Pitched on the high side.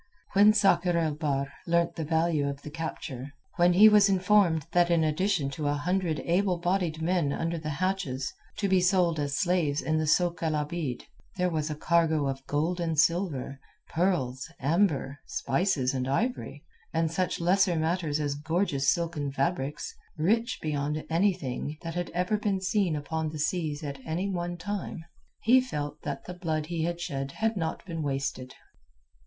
No: medium, 165 Hz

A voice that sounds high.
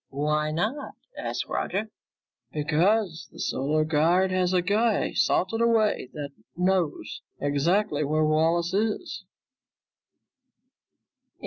No: medium, 175 Hz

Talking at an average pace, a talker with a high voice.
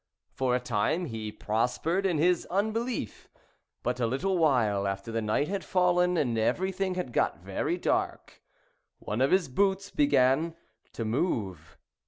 No: average, 150 wpm; medium, 140 Hz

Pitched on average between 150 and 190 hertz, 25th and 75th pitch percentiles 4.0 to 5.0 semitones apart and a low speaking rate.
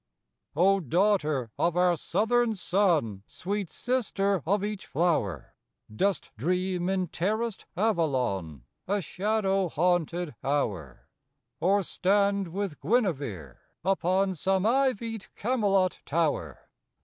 Yes: medium, 185 Hz; average, 4.5 semitones; slow, 100 wpm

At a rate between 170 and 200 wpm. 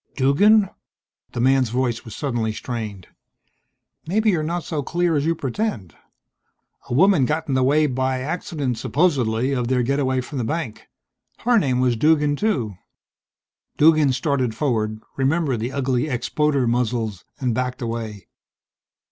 No: average, 145 wpm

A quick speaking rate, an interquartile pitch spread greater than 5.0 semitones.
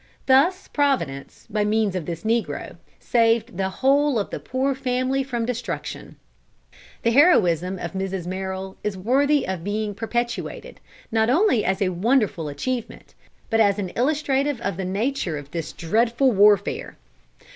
No: average, 145 wpm; wide, 5.5 semitones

